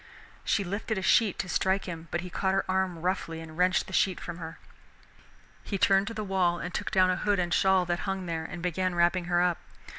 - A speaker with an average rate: No, fast, 235 wpm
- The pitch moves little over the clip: Yes, narrow, 1.7 semitones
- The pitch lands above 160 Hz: Yes, medium, 185 Hz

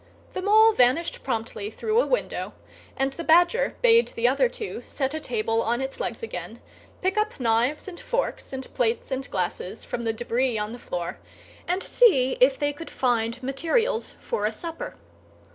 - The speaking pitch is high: Yes, very high, 270 Hz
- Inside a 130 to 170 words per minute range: No, average, 180 wpm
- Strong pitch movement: Yes, wide, 8.4 semitones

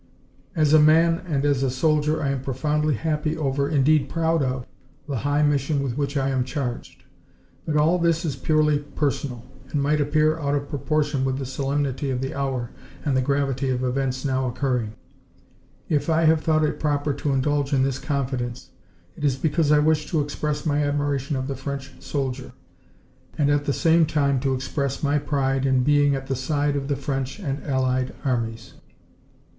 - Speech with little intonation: Yes, narrow, 2.1 semitones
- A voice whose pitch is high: No, medium, 140 Hz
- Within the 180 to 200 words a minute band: Yes, average, 185 wpm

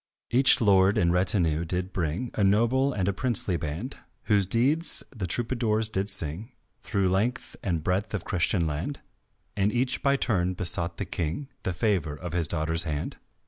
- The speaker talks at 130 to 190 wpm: Yes, average, 170 wpm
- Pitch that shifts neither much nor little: Yes, average, 4.9 semitones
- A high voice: No, very low, 95 Hz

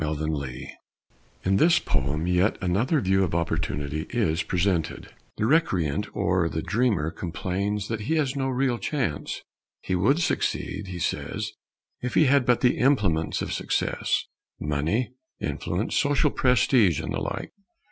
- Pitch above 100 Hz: No, very low, 95 Hz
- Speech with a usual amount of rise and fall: No, wide, 7.2 semitones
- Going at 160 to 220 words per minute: No, average, 145 wpm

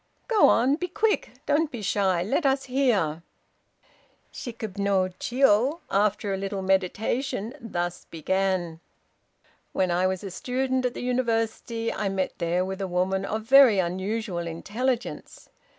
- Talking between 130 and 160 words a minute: Yes, average, 140 wpm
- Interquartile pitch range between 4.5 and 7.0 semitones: Yes, average, 5.1 semitones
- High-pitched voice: Yes, high, 205 Hz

